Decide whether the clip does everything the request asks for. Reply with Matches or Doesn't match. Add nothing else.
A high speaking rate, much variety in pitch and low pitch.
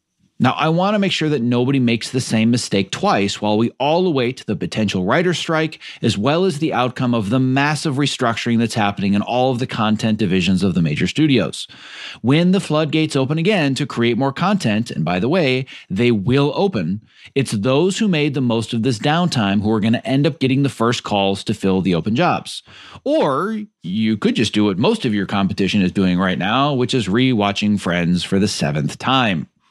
Matches